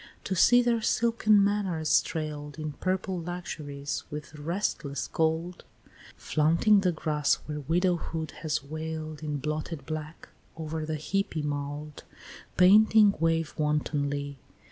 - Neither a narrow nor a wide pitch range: Yes, average, 3.3 semitones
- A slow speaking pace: Yes, slow, 120 wpm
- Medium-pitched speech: Yes, medium, 160 Hz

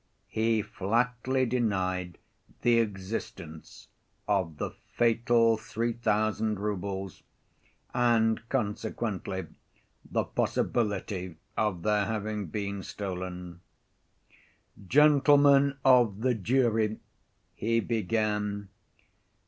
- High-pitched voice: No, low, 110 Hz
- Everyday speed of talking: No, slow, 80 wpm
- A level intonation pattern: No, average, 3.2 semitones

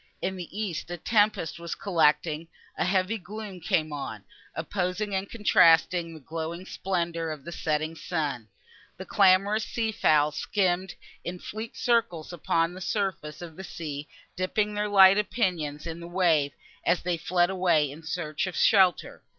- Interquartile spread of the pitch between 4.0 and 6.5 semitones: No, average, 3.3 semitones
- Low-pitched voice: No, medium, 175 Hz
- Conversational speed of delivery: Yes, average, 160 wpm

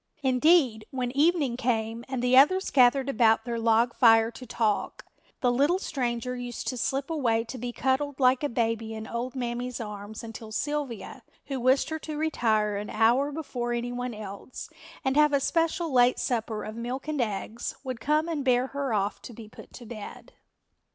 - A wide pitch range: No, average, 3.3 semitones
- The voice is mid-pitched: No, high, 245 Hz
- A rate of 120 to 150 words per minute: No, average, 185 wpm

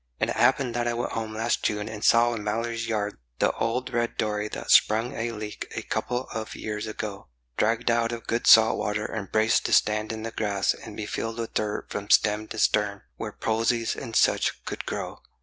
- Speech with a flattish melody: Yes, narrow, 1.6 semitones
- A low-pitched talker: Yes, low, 110 Hz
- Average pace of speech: No, fast, 215 wpm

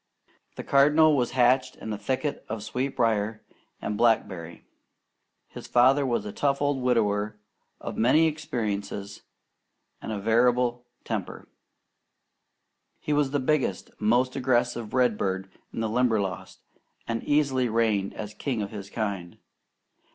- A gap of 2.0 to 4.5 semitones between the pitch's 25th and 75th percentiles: Yes, average, 3.8 semitones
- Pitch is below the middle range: Yes, low, 120 Hz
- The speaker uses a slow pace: Yes, slow, 120 wpm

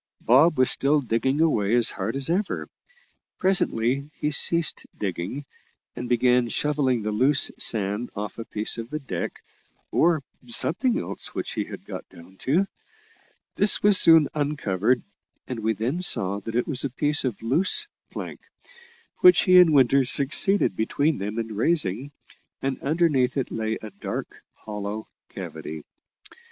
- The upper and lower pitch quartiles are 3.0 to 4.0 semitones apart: No, wide, 5.5 semitones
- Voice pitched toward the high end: No, low, 130 Hz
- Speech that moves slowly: No, average, 150 wpm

